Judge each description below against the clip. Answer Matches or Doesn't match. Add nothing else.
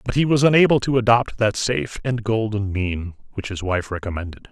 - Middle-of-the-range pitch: Doesn't match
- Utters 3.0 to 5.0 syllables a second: Doesn't match